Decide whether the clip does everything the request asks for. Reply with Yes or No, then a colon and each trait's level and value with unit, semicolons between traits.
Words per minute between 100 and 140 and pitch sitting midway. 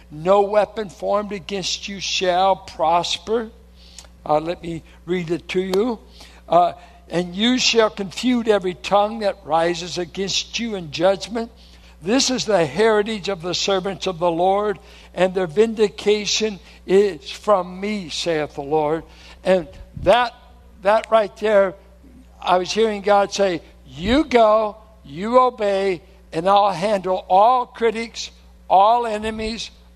No: slow, 135 wpm; high, 195 Hz